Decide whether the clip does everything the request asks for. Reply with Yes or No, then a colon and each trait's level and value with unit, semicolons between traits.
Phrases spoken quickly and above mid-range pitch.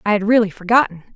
Yes: fast, 210 wpm; high, 210 Hz